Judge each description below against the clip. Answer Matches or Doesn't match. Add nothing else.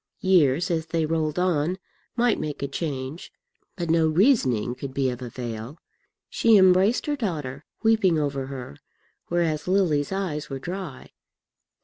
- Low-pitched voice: Doesn't match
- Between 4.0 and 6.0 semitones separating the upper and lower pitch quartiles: Matches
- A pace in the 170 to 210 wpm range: Doesn't match